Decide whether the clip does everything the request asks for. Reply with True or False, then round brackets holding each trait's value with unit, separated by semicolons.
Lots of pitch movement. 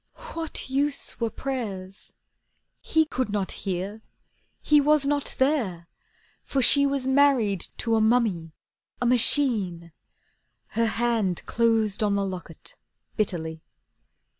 True (5.9 semitones)